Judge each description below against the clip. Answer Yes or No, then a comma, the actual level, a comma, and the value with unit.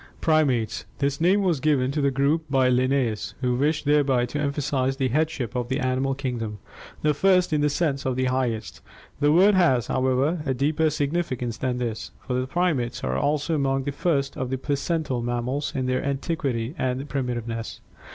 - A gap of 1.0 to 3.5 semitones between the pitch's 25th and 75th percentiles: Yes, average, 2.9 semitones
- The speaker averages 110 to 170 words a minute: No, average, 180 wpm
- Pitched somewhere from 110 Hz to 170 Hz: Yes, low, 135 Hz